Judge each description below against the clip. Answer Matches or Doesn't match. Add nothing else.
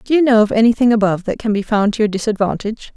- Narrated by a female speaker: Matches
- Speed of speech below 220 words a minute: Doesn't match